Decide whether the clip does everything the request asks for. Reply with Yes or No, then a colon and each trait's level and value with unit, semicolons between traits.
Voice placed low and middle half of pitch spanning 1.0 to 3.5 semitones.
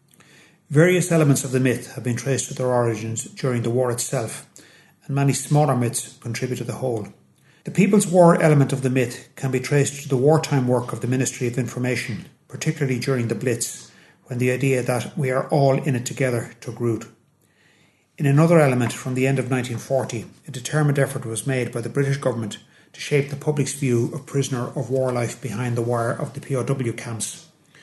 Yes: low, 130 Hz; average, 2.7 semitones